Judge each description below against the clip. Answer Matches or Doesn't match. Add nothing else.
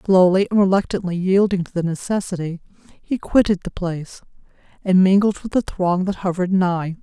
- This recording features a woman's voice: Matches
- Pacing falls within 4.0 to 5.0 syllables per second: Doesn't match